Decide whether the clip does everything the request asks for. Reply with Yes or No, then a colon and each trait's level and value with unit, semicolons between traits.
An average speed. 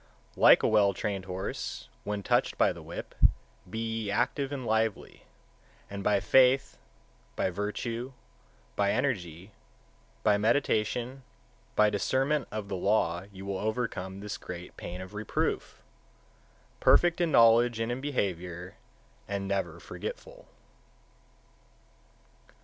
No: slow, 125 wpm